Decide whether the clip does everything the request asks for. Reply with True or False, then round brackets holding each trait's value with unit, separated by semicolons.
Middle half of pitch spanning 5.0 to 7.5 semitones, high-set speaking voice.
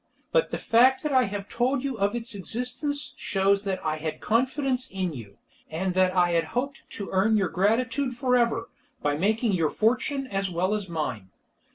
True (5.3 semitones; 210 Hz)